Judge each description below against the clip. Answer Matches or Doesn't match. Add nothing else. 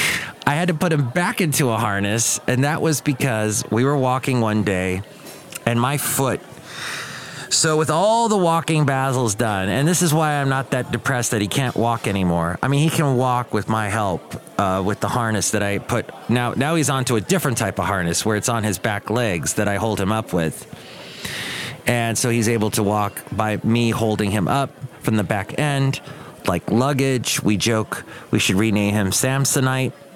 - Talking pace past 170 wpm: Matches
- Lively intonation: Doesn't match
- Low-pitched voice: Matches